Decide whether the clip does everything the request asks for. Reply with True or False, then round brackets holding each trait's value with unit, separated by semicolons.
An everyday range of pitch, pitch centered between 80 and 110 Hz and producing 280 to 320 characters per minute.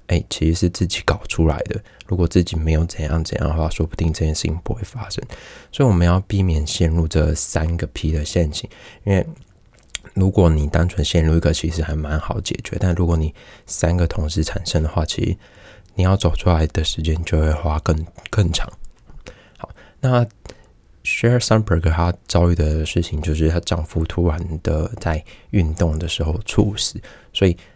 True (3.6 semitones; 85 Hz; 290 characters per minute)